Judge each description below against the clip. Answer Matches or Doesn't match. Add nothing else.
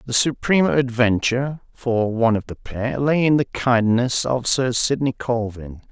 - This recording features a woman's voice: Doesn't match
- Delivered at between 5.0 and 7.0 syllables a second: Doesn't match